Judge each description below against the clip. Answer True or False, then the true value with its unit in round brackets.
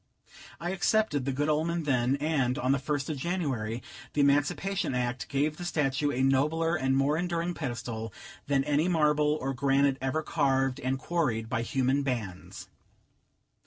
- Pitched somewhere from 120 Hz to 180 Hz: True (140 Hz)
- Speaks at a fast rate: False (160 wpm)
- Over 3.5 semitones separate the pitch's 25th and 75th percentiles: False (2.9 semitones)